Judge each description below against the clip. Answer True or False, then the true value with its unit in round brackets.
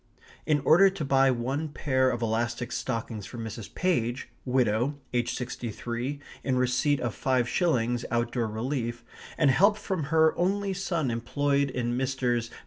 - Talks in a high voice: False (130 Hz)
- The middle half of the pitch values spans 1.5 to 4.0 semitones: True (3.5 semitones)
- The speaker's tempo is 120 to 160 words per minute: True (155 wpm)